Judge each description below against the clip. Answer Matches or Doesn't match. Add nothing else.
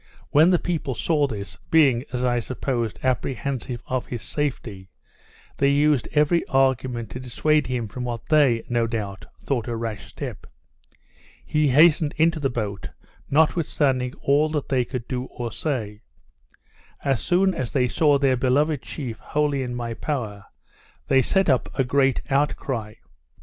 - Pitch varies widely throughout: Doesn't match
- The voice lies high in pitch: Doesn't match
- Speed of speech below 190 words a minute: Matches